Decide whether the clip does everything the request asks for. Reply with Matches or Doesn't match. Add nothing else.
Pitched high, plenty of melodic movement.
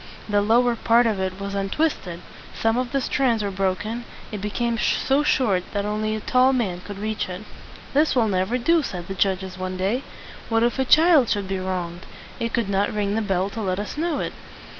Doesn't match